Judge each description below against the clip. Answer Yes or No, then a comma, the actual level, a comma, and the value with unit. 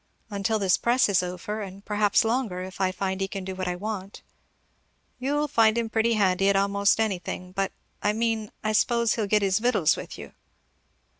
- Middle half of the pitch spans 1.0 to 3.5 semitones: Yes, average, 2.8 semitones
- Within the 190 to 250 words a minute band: Yes, average, 200 wpm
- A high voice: Yes, high, 205 Hz